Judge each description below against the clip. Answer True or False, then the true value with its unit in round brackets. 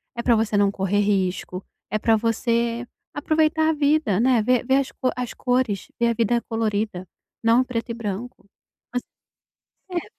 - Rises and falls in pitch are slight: False (3.3 semitones)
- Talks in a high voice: True (230 Hz)